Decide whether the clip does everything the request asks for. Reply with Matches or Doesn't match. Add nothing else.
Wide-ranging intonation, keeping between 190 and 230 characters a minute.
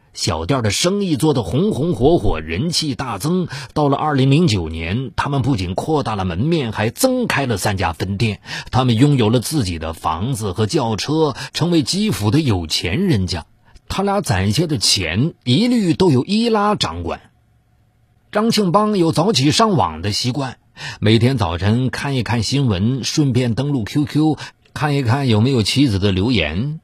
Doesn't match